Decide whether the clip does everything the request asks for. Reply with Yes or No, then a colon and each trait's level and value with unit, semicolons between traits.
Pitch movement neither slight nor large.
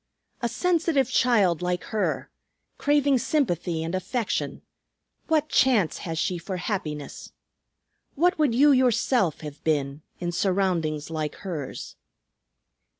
No: wide, 8.2 semitones